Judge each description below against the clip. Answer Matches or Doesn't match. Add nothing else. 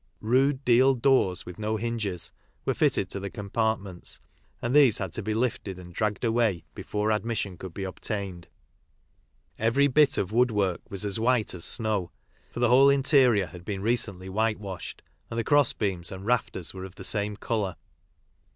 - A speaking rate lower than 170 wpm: Doesn't match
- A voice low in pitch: Matches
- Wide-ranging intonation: Doesn't match